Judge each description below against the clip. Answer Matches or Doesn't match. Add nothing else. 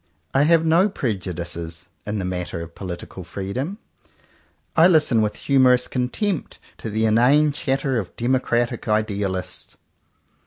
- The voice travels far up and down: Matches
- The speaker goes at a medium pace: Doesn't match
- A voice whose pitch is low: Matches